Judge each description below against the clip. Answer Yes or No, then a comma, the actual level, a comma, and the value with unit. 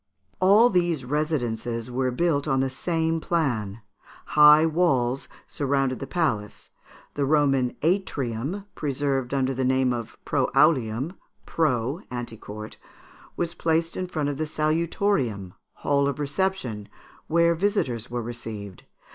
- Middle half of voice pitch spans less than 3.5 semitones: No, average, 5.0 semitones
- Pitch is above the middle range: No, medium, 140 Hz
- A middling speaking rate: No, slow, 125 wpm